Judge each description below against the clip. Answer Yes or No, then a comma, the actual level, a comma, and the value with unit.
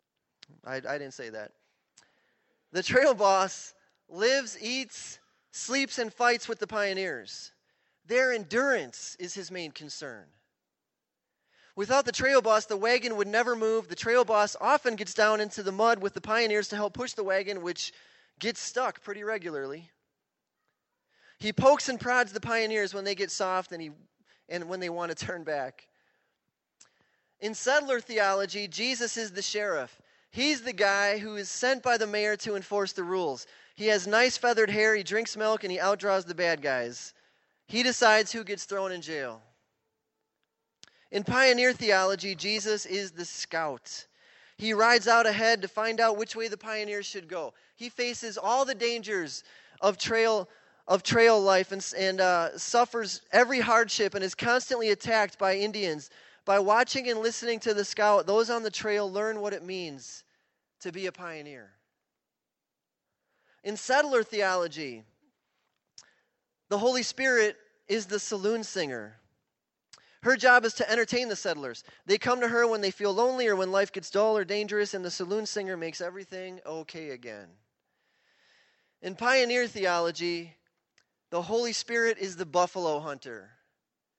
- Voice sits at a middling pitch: No, high, 210 Hz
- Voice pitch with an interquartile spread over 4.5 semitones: No, average, 3.7 semitones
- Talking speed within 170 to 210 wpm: No, average, 160 wpm